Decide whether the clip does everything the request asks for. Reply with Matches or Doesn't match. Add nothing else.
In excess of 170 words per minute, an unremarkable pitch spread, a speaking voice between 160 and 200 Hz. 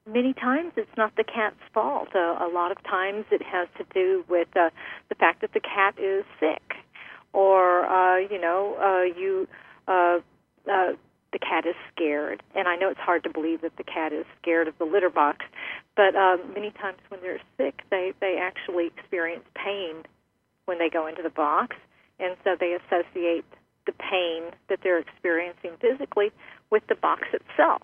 Matches